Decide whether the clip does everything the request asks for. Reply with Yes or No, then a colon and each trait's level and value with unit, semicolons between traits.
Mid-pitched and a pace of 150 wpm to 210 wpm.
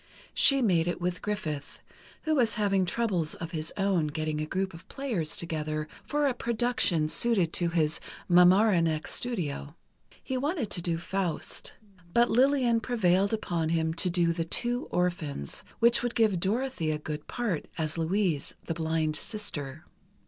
Yes: medium, 180 Hz; average, 155 wpm